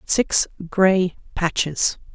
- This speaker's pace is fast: No, slow, 85 wpm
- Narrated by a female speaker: Yes, female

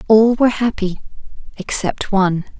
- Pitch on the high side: Yes, high, 210 Hz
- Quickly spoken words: No, slow, 115 wpm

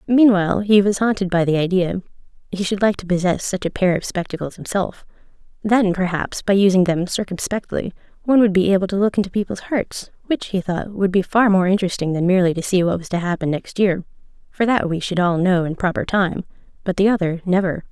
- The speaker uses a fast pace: Yes, fast, 210 wpm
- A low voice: No, high, 190 Hz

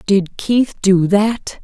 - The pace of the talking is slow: Yes, slow, 110 wpm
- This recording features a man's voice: No, female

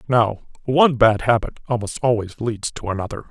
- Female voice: No, male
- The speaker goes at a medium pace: Yes, average, 165 wpm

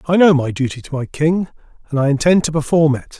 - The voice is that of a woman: No, male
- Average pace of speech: No, fast, 245 wpm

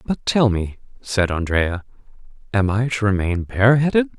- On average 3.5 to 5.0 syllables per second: Yes, 4.8 syllables/s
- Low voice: Yes, low, 110 Hz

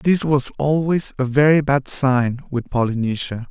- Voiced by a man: Yes, male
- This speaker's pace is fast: No, average, 155 wpm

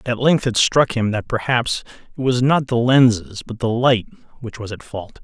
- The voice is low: Yes, low, 120 Hz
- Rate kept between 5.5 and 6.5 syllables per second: No, 4.7 syllables/s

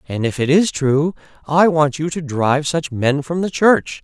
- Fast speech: Yes, fast, 225 wpm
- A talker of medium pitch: Yes, medium, 150 Hz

